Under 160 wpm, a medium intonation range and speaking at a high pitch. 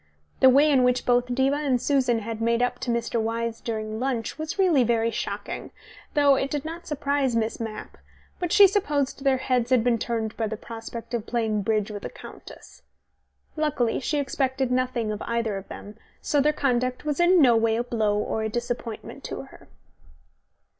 No: average, 195 wpm; average, 3.5 semitones; high, 245 Hz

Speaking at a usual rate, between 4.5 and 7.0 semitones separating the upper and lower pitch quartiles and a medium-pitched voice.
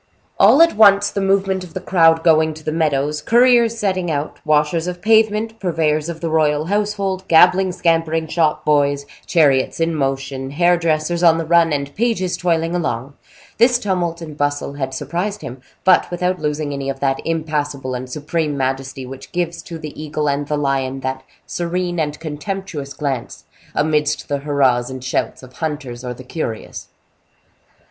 No: average, 170 wpm; average, 3.8 semitones; medium, 155 Hz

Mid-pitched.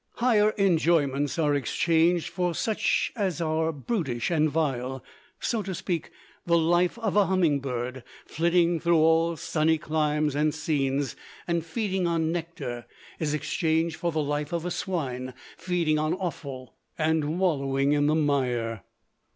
Yes: medium, 160 Hz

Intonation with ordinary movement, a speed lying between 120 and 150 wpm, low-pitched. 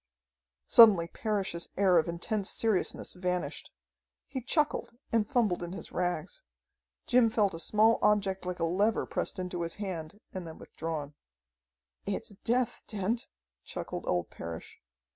No: average, 4.2 semitones; average, 140 wpm; high, 190 Hz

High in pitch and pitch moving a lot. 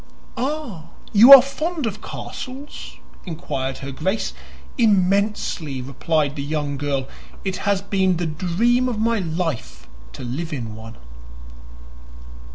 No: medium, 180 Hz; wide, 7.7 semitones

